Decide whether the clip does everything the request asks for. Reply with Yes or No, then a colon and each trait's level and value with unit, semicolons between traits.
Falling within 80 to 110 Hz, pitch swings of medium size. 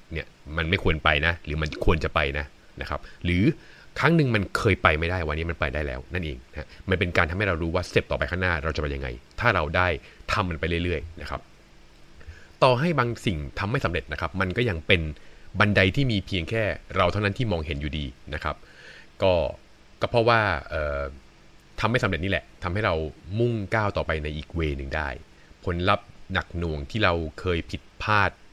Yes: very low, 85 Hz; average, 5.0 semitones